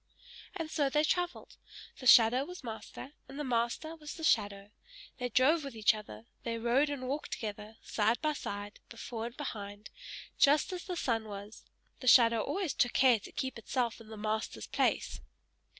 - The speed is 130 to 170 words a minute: No, average, 180 wpm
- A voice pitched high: Yes, high, 240 Hz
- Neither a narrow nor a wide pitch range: Yes, average, 4.9 semitones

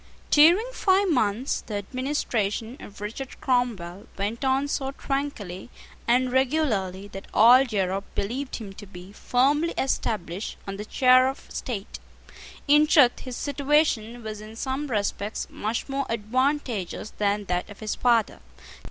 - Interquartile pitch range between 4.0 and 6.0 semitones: Yes, average, 4.9 semitones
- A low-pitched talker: No, high, 235 Hz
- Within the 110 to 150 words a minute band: Yes, average, 140 wpm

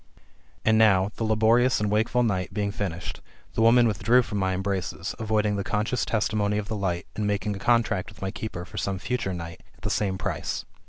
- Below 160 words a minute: No, fast, 205 wpm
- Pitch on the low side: Yes, low, 105 Hz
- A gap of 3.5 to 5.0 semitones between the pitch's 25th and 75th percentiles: No, narrow, 2.5 semitones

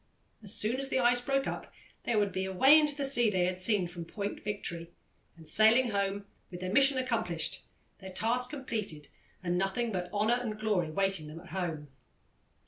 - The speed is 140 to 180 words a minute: No, average, 190 wpm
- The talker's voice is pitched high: Yes, high, 205 Hz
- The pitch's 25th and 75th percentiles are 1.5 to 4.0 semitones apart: No, average, 5.1 semitones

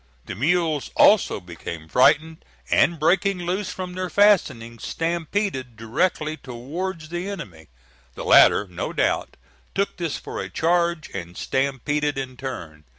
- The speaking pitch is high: No, medium, 155 Hz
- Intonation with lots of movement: Yes, wide, 6.8 semitones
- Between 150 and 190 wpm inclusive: No, slow, 135 wpm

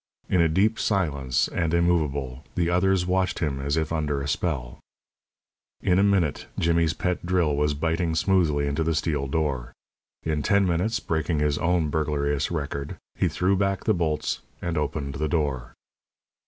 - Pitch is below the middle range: Yes, very low, 80 Hz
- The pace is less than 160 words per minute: No, average, 165 wpm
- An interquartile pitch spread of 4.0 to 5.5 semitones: No, average, 3.5 semitones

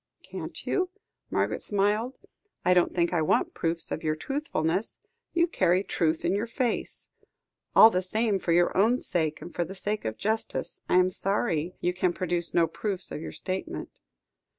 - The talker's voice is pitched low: No, medium, 185 Hz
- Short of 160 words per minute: No, average, 175 wpm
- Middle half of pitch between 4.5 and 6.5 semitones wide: No, average, 3.9 semitones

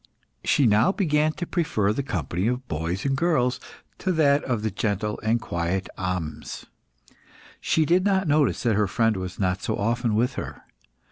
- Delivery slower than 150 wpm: No, average, 175 wpm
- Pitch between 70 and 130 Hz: Yes, low, 115 Hz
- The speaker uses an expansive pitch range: Yes, wide, 7.0 semitones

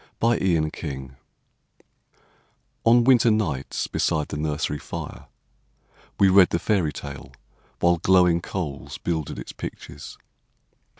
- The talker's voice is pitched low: Yes, very low, 85 Hz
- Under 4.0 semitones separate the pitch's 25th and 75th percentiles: No, average, 4.8 semitones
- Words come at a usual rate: No, slow, 115 wpm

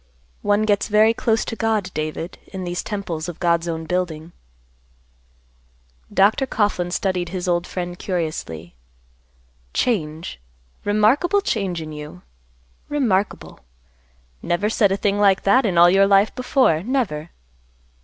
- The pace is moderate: No, slow, 130 wpm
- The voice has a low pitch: No, high, 190 Hz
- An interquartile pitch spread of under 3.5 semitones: No, average, 3.8 semitones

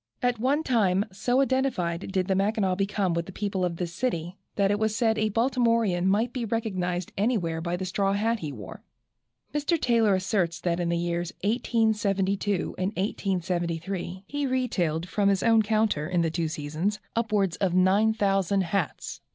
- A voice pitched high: Yes, high, 195 Hz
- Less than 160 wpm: No, average, 170 wpm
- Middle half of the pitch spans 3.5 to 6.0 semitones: Yes, average, 3.9 semitones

